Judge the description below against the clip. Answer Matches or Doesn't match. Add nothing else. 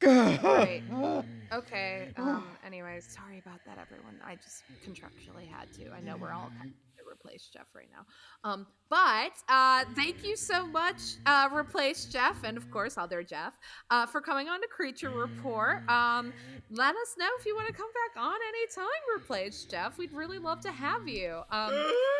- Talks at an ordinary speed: Matches